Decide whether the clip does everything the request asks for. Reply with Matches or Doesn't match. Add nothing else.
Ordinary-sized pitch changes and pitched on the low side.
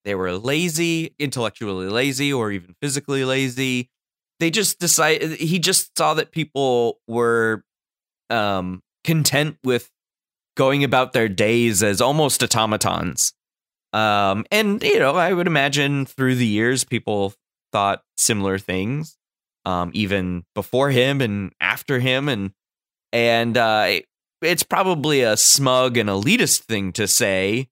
Doesn't match